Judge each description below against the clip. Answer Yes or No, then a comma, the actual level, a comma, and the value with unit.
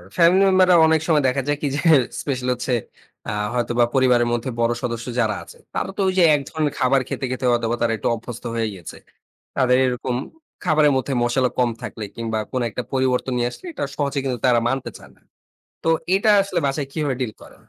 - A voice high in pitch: No, low, 130 Hz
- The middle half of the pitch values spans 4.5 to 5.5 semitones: No, average, 3.4 semitones